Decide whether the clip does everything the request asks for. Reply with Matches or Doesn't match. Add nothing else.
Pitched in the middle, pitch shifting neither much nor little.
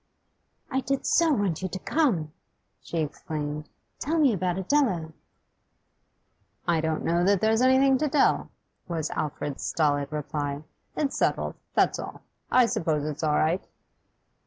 Doesn't match